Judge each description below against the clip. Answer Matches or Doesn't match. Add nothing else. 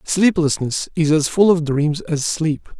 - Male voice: Matches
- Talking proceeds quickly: Doesn't match